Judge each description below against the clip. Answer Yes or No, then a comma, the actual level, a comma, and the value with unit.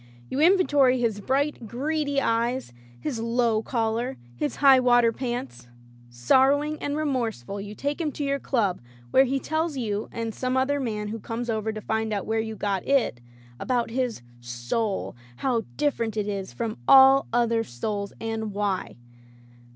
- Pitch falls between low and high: No, high, 230 Hz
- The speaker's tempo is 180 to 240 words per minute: No, average, 165 wpm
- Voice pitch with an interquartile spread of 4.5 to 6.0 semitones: No, average, 4.1 semitones